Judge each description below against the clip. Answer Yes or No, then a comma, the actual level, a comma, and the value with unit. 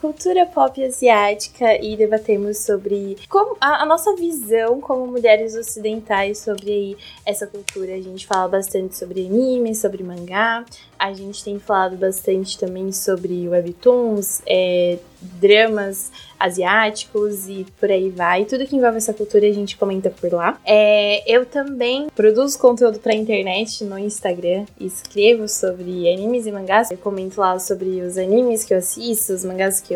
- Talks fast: No, average, 155 wpm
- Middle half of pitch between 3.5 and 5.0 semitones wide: No, average, 3.1 semitones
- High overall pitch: Yes, high, 205 Hz